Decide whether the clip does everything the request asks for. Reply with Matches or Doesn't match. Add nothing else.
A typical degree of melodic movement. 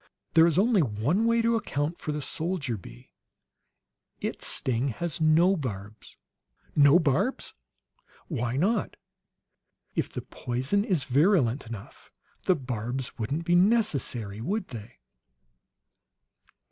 Doesn't match